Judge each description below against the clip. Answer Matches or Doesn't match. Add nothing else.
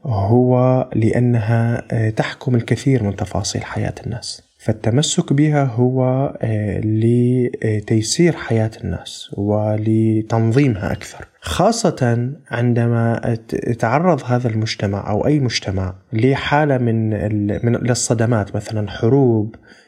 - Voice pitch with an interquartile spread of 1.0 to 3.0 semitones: Matches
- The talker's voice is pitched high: Doesn't match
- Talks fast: Doesn't match